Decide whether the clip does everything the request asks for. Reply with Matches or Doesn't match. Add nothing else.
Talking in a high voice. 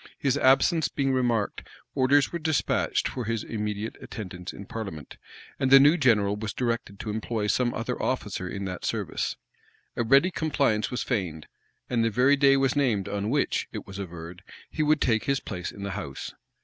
Doesn't match